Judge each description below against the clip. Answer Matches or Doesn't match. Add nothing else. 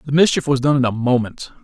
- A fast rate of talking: Matches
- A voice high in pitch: Doesn't match